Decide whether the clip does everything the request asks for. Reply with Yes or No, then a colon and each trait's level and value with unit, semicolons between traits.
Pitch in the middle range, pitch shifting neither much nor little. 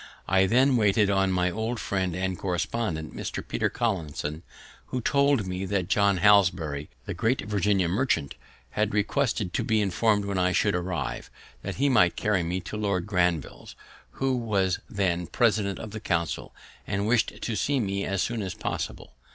No: low, 100 Hz; average, 3.3 semitones